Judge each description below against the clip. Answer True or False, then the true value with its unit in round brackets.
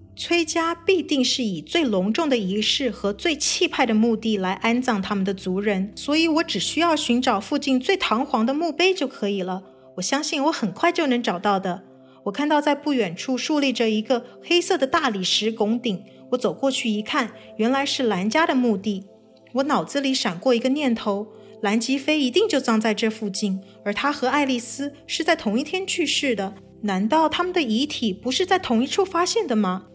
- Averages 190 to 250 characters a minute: False (290 characters per minute)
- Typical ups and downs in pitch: False (5.8 semitones)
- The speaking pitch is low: False (250 Hz)